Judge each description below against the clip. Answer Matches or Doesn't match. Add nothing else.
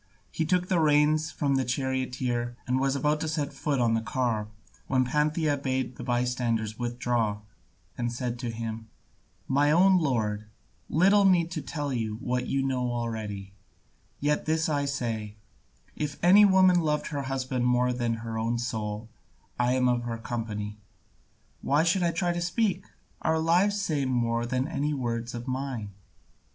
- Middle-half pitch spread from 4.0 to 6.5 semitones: Matches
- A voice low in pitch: Matches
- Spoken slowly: Doesn't match